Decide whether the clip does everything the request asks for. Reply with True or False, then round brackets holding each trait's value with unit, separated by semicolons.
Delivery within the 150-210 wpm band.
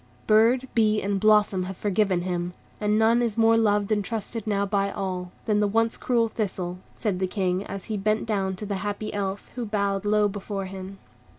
True (200 wpm)